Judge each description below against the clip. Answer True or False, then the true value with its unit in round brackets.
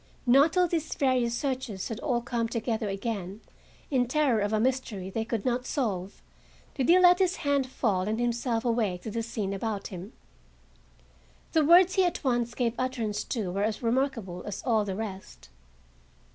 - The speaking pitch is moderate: False (235 Hz)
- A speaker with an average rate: True (175 wpm)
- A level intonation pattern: False (4.0 semitones)